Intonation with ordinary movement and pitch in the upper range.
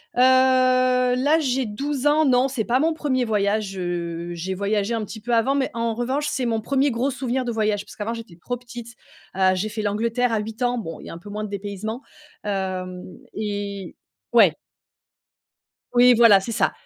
Yes: average, 3.6 semitones; high, 225 Hz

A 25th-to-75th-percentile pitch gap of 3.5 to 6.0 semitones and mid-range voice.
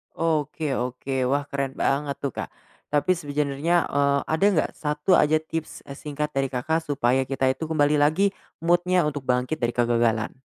No: narrow, 2.6 semitones; medium, 145 Hz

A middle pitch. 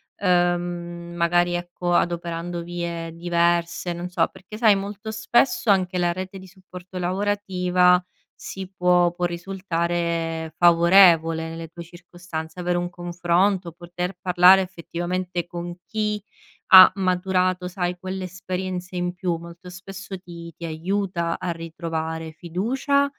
Yes: medium, 175 Hz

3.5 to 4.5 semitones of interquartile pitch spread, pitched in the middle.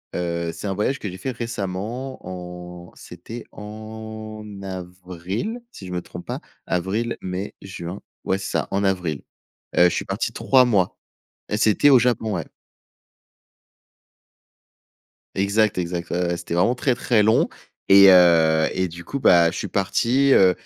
No: average, 3.8 semitones; very low, 95 Hz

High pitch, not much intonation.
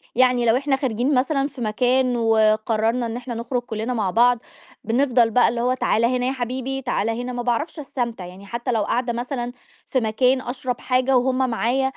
Yes: high, 245 Hz; narrow, 2.0 semitones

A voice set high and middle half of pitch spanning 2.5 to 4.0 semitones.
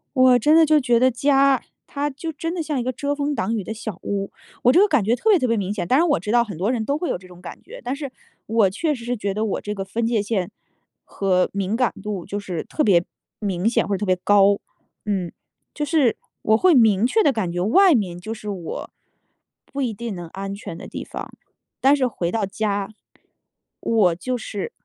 No: high, 225 Hz; wide, 5.6 semitones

